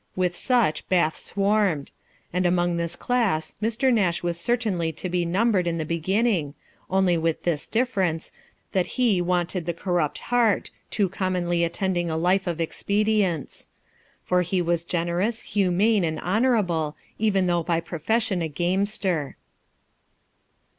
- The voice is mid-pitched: Yes, medium, 180 Hz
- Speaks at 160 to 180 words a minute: No, average, 140 wpm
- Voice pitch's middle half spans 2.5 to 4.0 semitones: Yes, average, 3.3 semitones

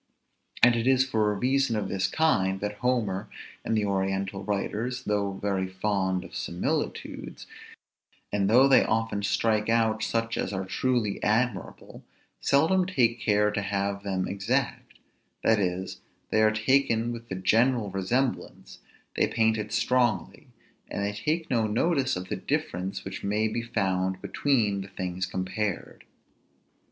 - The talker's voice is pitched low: Yes, low, 105 Hz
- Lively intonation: No, average, 3.5 semitones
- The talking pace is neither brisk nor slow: Yes, average, 150 wpm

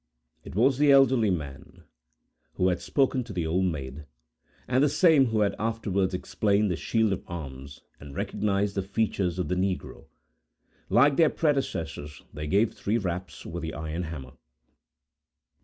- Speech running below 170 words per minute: Yes, average, 155 wpm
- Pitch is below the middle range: Yes, very low, 95 Hz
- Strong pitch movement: Yes, wide, 5.8 semitones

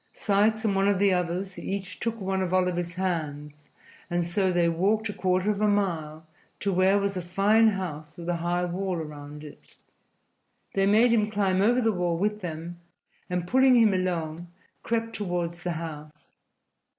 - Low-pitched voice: No, medium, 185 Hz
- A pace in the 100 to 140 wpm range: No, average, 175 wpm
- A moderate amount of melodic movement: Yes, average, 3.0 semitones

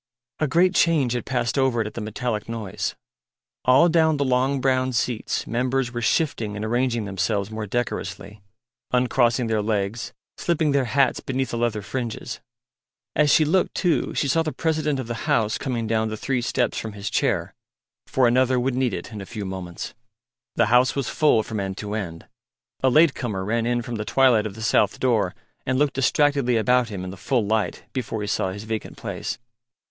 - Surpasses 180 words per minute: Yes, average, 195 wpm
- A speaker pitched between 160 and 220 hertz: No, low, 120 Hz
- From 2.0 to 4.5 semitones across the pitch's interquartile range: Yes, average, 3.6 semitones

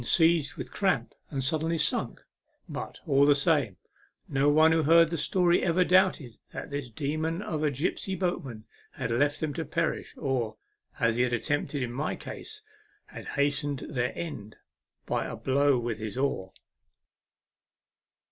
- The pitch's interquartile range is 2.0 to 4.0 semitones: No, average, 4.4 semitones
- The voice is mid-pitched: Yes, medium, 145 Hz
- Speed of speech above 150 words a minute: Yes, average, 160 wpm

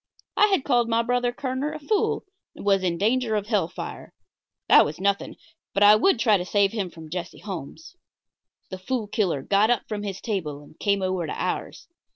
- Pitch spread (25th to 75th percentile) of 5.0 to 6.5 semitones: No, average, 4.5 semitones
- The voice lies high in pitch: Yes, high, 205 Hz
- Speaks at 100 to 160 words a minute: No, average, 200 wpm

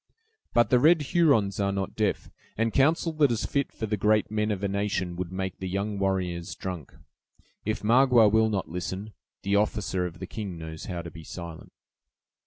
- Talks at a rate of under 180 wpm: No, average, 195 wpm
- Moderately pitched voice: No, low, 100 Hz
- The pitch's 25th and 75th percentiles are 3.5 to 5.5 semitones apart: No, average, 3.1 semitones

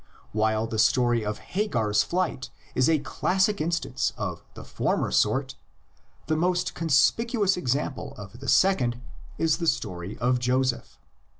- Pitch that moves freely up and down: Yes, wide, 6.8 semitones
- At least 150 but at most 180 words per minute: No, slow, 135 wpm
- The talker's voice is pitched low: Yes, low, 130 Hz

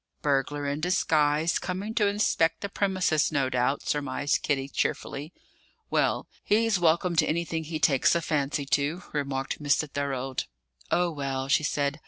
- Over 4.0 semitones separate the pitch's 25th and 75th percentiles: No, average, 3.4 semitones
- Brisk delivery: No, average, 150 wpm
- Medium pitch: Yes, medium, 150 Hz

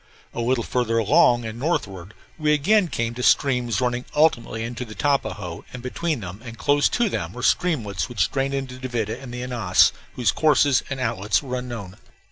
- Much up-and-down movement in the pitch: No, average, 3.5 semitones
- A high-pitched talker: No, low, 125 Hz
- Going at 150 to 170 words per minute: No, average, 185 wpm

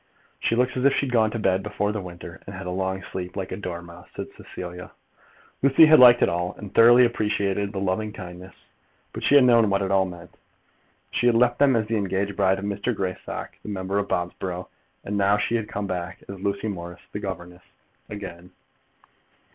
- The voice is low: Yes, low, 100 Hz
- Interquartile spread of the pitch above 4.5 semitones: No, average, 3.0 semitones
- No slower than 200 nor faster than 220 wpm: Yes, fast, 205 wpm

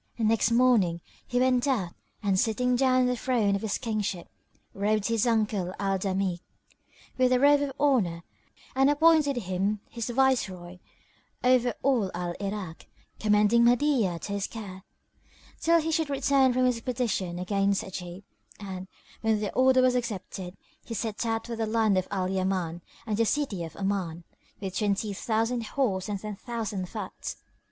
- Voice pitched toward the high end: Yes, high, 215 Hz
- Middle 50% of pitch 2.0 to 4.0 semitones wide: No, average, 4.6 semitones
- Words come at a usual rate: Yes, average, 160 wpm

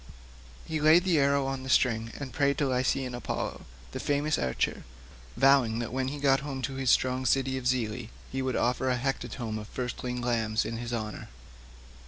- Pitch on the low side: Yes, low, 130 Hz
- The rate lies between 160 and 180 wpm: No, average, 190 wpm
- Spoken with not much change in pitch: Yes, narrow, 2.3 semitones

